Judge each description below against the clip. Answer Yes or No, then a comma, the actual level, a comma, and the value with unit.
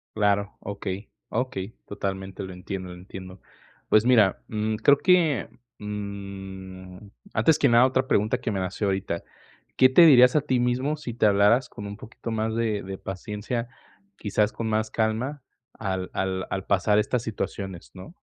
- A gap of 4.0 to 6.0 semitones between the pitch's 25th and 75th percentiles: No, average, 3.5 semitones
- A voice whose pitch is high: No, low, 105 Hz